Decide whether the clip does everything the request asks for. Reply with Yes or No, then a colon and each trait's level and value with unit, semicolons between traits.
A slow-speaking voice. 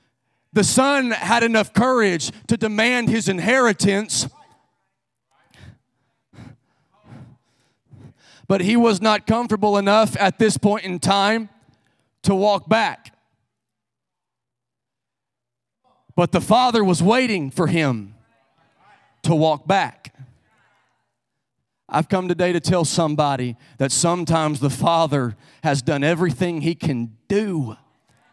Yes: slow, 105 wpm